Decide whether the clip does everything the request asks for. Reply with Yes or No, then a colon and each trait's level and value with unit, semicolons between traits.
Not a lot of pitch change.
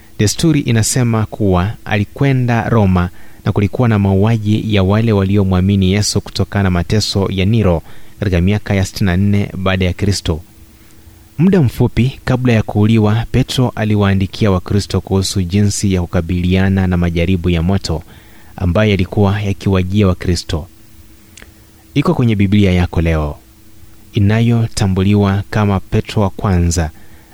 Yes: narrow, 2.3 semitones